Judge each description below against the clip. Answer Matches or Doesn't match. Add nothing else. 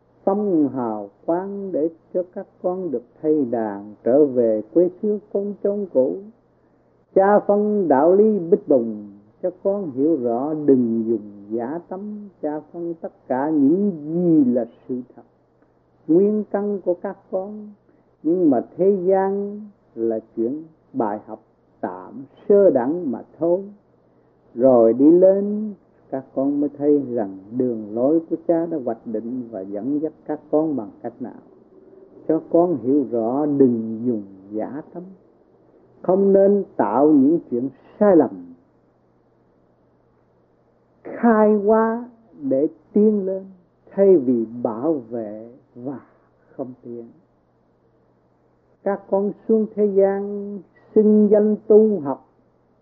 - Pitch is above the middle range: Doesn't match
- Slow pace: Matches